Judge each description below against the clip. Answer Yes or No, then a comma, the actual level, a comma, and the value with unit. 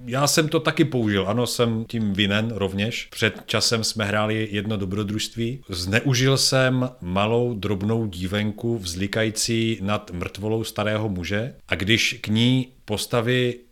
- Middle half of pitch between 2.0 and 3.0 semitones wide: Yes, narrow, 2.6 semitones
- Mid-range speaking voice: No, low, 110 Hz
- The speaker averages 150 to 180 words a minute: No, average, 135 wpm